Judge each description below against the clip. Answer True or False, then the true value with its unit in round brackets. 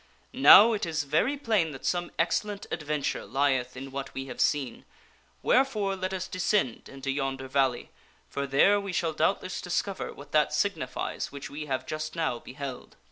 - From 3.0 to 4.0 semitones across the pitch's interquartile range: False (5.5 semitones)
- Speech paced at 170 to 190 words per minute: True (175 wpm)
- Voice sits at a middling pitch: True (150 Hz)